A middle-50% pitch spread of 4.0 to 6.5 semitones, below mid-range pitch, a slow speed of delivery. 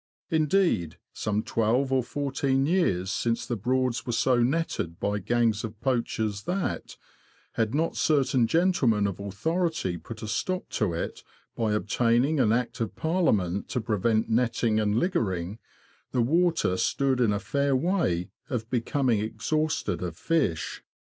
No: average, 5.1 semitones; low, 120 Hz; average, 145 wpm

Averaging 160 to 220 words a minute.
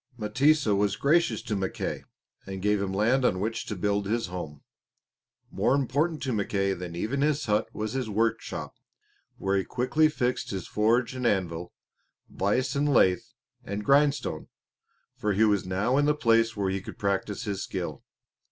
Yes: average, 170 wpm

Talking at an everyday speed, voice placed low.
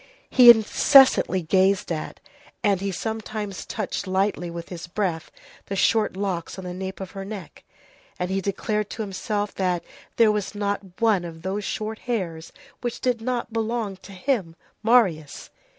No: average, 160 wpm; high, 200 Hz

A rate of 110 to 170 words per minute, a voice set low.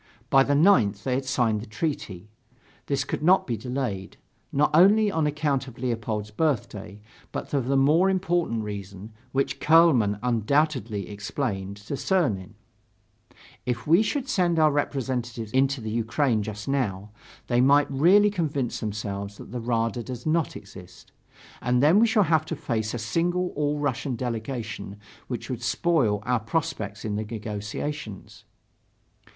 Yes: average, 155 wpm; low, 125 Hz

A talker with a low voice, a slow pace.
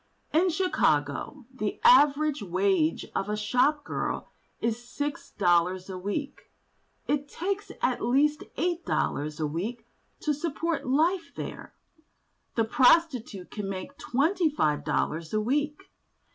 No: very high, 255 Hz; slow, 130 wpm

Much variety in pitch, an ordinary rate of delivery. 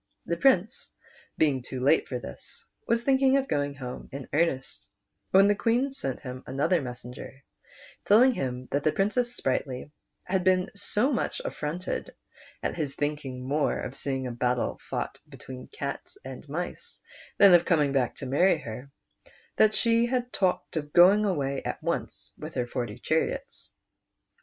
Yes: wide, 7.3 semitones; average, 160 wpm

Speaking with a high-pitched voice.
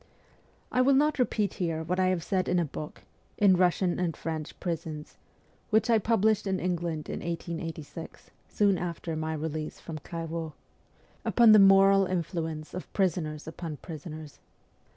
No: medium, 170 Hz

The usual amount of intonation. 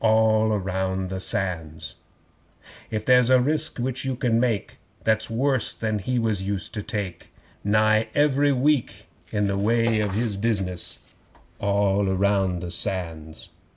Yes: average, 3.6 semitones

